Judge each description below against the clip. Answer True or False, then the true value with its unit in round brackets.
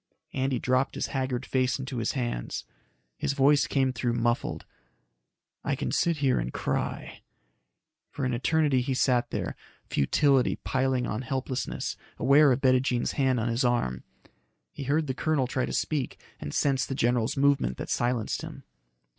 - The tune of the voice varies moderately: False (2.1 semitones)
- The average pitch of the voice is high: False (130 Hz)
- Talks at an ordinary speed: True (160 wpm)